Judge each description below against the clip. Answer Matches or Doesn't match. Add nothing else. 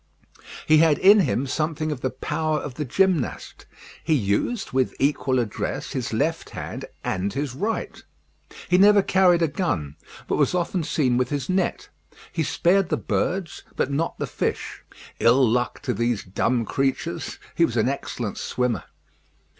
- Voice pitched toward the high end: Doesn't match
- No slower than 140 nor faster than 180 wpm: Matches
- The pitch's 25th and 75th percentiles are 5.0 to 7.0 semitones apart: Matches